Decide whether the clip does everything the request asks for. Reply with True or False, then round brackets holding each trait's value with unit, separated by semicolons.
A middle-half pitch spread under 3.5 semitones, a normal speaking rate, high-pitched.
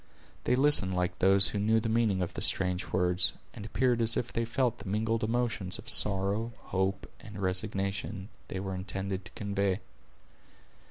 False (2.9 semitones; 170 wpm; 100 Hz)